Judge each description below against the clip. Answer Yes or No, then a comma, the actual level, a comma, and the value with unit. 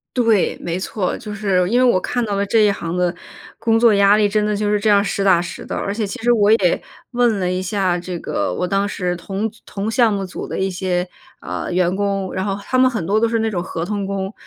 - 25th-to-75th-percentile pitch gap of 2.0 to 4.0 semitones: Yes, average, 2.8 semitones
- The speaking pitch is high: Yes, high, 200 Hz